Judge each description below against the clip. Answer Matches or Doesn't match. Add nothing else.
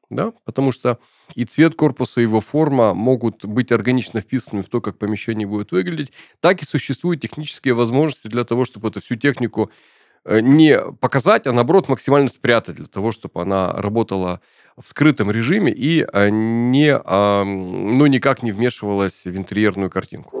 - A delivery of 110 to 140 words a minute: Doesn't match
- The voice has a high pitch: Doesn't match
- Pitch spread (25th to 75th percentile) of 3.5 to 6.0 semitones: Matches